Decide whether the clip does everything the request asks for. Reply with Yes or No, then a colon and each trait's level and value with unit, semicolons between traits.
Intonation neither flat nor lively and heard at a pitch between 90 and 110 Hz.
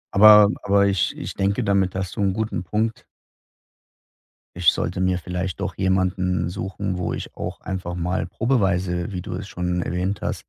No: narrow, 1.9 semitones; very low, 95 Hz